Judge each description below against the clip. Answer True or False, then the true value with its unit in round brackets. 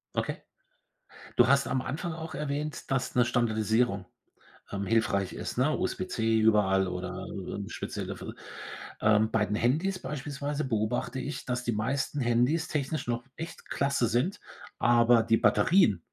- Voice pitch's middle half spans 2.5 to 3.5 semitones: False (4.6 semitones)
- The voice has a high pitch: False (125 Hz)